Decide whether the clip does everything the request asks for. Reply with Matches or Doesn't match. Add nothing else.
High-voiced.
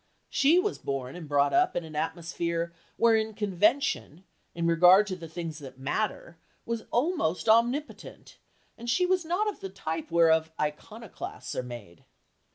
Doesn't match